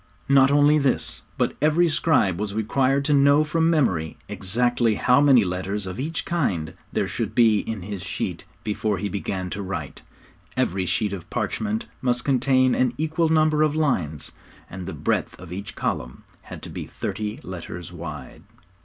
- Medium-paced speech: Yes, average, 170 wpm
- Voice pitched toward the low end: Yes, low, 115 Hz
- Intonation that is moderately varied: No, wide, 7.5 semitones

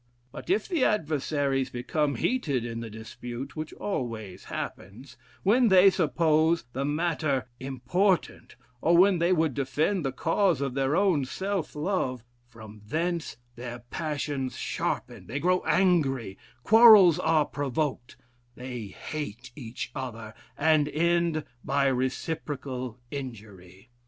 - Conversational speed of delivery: No, slow, 125 wpm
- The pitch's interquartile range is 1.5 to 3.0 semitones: No, average, 5.2 semitones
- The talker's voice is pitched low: No, medium, 145 Hz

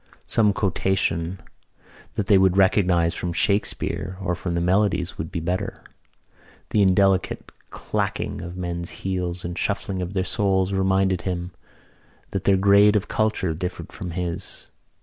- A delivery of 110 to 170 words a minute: Yes, average, 150 wpm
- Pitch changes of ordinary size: No, narrow, 1.9 semitones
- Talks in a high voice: No, very low, 95 Hz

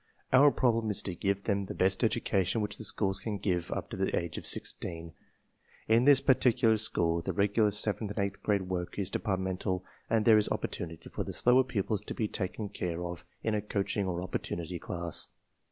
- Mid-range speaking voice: No, low, 100 Hz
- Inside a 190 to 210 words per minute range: Yes, average, 200 wpm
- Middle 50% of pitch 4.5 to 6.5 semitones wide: No, average, 3.3 semitones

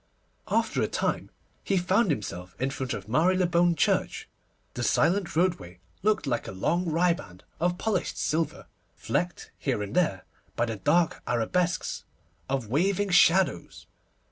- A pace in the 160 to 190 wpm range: No, average, 140 wpm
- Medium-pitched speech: Yes, medium, 165 Hz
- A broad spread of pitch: Yes, wide, 6.9 semitones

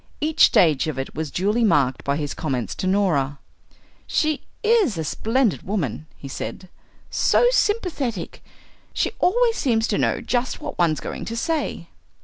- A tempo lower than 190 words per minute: Yes, average, 155 wpm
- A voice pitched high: Yes, high, 200 Hz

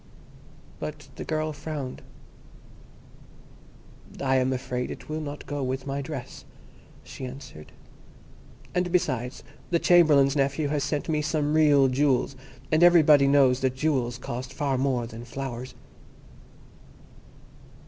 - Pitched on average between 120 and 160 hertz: Yes, medium, 140 Hz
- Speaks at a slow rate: Yes, slow, 125 wpm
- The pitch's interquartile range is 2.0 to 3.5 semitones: Yes, average, 2.9 semitones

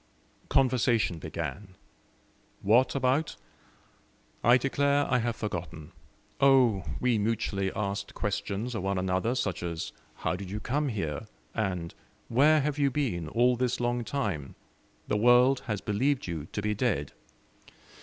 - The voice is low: Yes, low, 110 Hz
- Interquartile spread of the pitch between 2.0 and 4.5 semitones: No, average, 4.9 semitones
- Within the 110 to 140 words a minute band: Yes, slow, 135 wpm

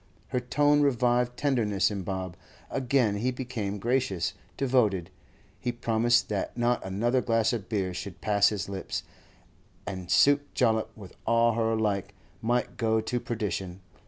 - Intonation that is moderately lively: Yes, average, 3.6 semitones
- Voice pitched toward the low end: Yes, low, 115 Hz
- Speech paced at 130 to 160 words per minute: Yes, average, 145 wpm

